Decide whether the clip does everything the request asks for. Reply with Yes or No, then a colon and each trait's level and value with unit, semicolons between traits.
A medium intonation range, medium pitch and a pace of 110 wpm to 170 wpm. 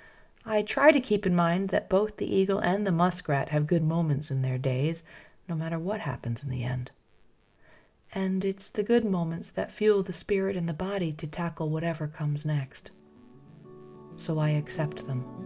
No: average, 4.8 semitones; medium, 165 Hz; average, 185 wpm